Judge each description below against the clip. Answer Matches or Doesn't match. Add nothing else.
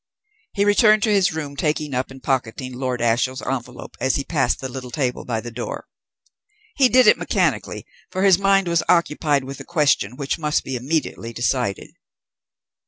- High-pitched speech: Doesn't match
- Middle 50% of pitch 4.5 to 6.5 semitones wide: Matches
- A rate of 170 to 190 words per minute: Matches